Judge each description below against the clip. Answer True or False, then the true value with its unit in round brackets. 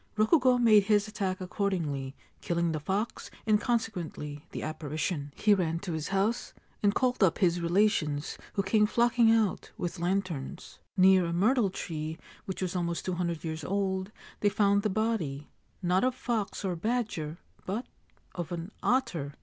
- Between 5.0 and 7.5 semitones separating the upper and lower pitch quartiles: False (4.2 semitones)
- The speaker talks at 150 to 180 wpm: True (165 wpm)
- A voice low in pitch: False (190 Hz)